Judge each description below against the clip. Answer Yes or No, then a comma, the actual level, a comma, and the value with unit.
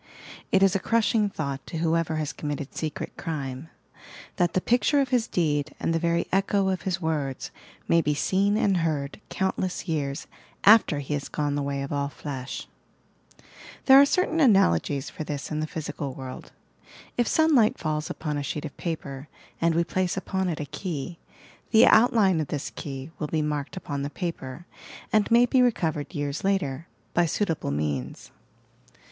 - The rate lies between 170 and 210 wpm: Yes, average, 180 wpm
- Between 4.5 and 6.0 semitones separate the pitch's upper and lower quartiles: Yes, average, 5.0 semitones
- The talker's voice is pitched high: No, medium, 160 Hz